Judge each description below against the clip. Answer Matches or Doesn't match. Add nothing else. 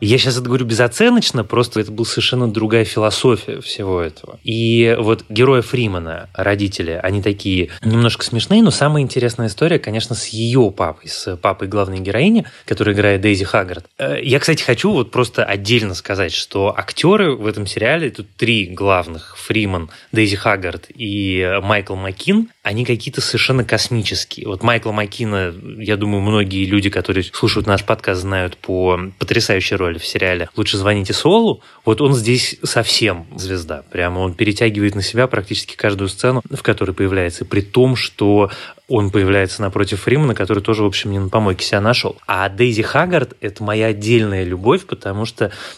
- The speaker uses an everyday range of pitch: Matches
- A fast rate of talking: Matches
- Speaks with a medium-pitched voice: Doesn't match